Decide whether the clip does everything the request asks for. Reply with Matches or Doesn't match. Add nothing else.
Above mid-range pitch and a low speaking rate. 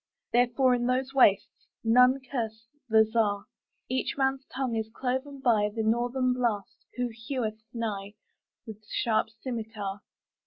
Matches